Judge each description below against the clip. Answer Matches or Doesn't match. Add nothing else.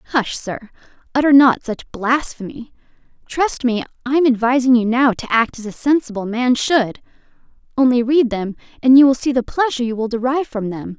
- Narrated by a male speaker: Doesn't match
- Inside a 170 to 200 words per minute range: Matches